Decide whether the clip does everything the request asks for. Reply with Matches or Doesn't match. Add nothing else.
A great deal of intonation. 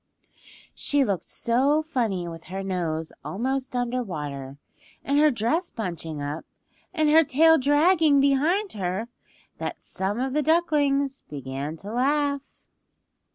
Matches